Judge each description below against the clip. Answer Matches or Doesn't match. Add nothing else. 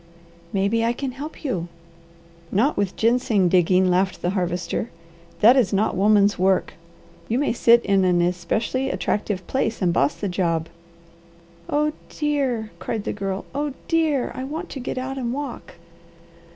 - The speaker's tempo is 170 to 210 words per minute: Doesn't match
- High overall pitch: Matches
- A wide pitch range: Matches